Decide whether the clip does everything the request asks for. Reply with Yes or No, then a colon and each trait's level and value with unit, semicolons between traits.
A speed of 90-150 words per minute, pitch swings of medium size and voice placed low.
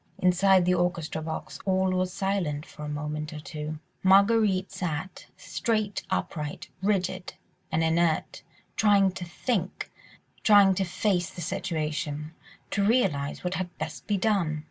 No: average, 140 wpm; average, 3.7 semitones; medium, 180 Hz